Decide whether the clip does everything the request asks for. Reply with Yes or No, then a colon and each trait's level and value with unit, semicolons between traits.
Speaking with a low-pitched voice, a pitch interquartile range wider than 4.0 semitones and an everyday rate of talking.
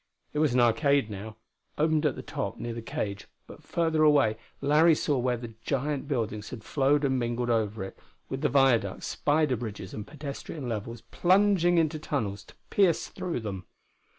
Yes: low, 130 Hz; average, 5.2 semitones; average, 180 wpm